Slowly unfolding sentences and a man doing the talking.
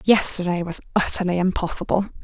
No: slow, 110 wpm; female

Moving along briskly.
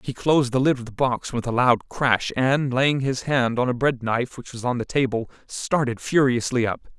Yes: fast, 230 wpm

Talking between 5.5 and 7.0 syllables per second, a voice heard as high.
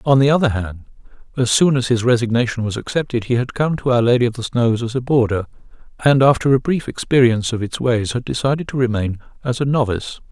No: 6.2 syllables/s; low, 120 Hz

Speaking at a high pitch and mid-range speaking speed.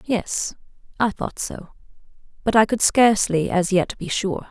Yes: high, 200 Hz; average, 160 wpm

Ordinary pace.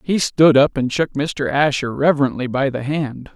Yes: average, 195 wpm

